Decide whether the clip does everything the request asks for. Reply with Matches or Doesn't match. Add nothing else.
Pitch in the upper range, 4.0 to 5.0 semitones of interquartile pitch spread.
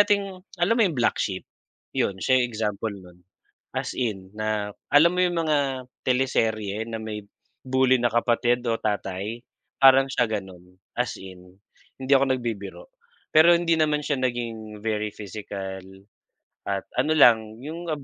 Doesn't match